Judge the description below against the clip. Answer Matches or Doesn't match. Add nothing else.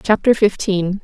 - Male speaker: Doesn't match